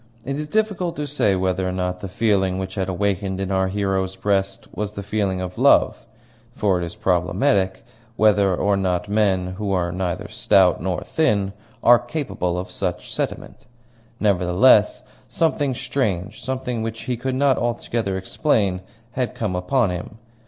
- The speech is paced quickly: No, average, 165 wpm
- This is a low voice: Yes, low, 100 Hz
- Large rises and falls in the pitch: No, average, 4.0 semitones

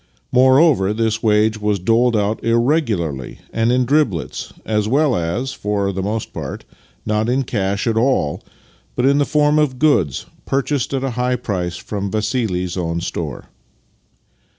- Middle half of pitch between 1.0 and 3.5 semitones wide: No, average, 4.7 semitones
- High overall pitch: No, low, 110 Hz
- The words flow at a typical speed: Yes, average, 150 wpm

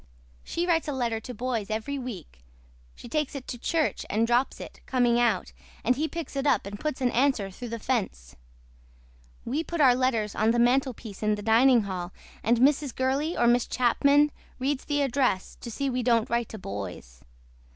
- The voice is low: No, high, 245 Hz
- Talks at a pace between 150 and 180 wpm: No, average, 195 wpm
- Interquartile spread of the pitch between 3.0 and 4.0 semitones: Yes, average, 3.7 semitones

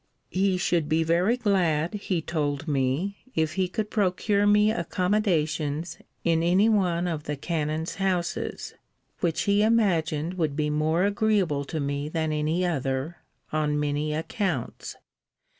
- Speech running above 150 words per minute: No, average, 140 wpm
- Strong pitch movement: No, average, 4.0 semitones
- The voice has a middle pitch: Yes, medium, 170 Hz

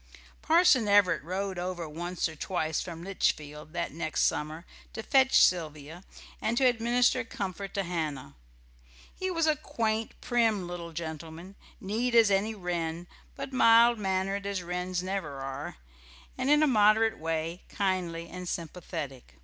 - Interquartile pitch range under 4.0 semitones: No, average, 5.1 semitones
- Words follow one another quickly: No, average, 145 wpm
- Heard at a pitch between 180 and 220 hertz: Yes, medium, 185 Hz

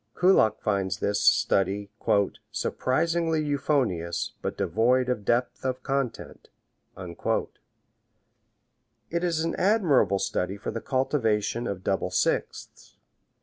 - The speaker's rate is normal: No, slow, 105 wpm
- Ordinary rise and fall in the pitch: No, wide, 6.4 semitones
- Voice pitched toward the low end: Yes, low, 120 Hz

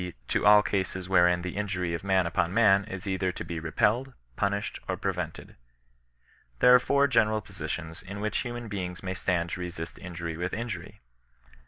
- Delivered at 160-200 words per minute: Yes, average, 175 wpm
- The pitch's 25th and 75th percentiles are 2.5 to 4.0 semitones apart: Yes, average, 3.0 semitones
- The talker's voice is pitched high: No, very low, 95 Hz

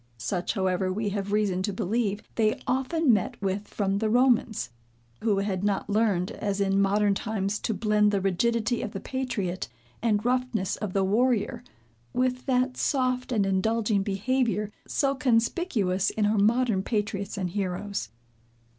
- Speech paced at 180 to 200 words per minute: No, average, 155 wpm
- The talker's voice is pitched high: Yes, high, 210 Hz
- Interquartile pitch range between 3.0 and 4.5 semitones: Yes, average, 3.3 semitones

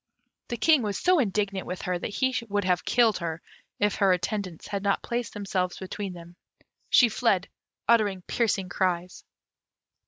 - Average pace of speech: Yes, average, 160 wpm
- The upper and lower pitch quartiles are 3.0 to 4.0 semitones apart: Yes, average, 3.3 semitones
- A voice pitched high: Yes, high, 200 Hz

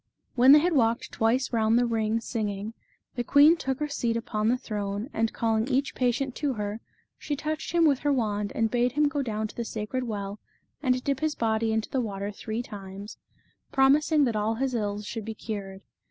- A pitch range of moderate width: Yes, average, 3.9 semitones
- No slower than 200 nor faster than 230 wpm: Yes, fast, 205 wpm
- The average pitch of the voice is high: Yes, high, 230 Hz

